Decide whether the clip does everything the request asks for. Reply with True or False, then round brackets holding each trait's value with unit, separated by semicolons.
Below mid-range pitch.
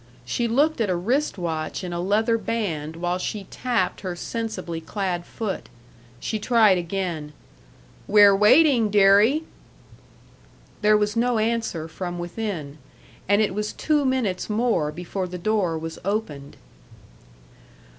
False (200 Hz)